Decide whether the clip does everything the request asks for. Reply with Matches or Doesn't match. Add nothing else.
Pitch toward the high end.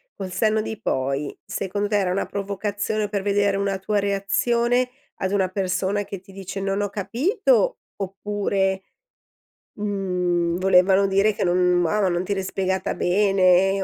Matches